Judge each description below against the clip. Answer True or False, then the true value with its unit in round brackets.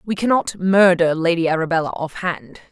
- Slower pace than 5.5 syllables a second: True (5.2 syllables/s)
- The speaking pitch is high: False (175 Hz)